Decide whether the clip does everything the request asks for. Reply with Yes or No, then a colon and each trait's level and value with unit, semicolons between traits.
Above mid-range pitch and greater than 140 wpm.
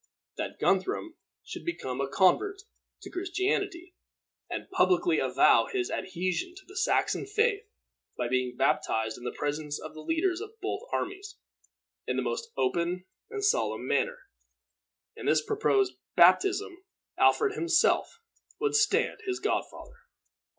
No: very high, 370 Hz; slow, 135 wpm